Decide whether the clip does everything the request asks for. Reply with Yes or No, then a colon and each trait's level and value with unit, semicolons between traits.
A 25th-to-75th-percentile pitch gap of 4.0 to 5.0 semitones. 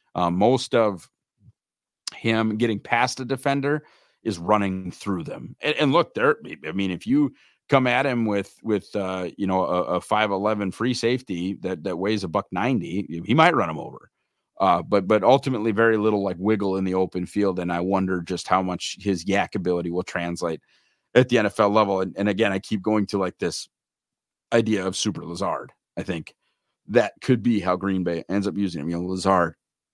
No: average, 2.9 semitones